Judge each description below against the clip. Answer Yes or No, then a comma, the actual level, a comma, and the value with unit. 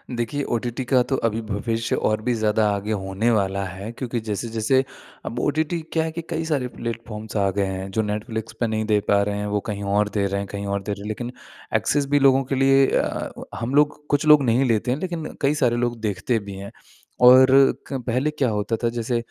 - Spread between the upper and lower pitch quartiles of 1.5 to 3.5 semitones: No, average, 4.2 semitones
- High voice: No, low, 115 Hz